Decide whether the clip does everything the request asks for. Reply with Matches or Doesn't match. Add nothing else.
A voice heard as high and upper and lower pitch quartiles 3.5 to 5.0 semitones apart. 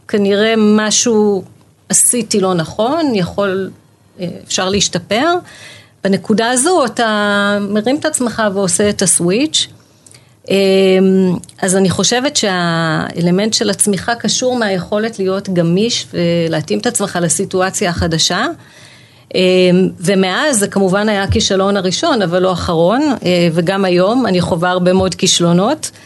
Doesn't match